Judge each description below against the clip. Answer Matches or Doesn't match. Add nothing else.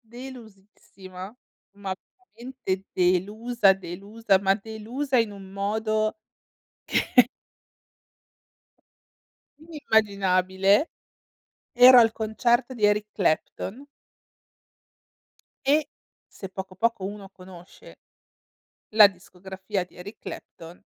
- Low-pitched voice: Doesn't match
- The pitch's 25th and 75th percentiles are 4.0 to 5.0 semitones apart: Doesn't match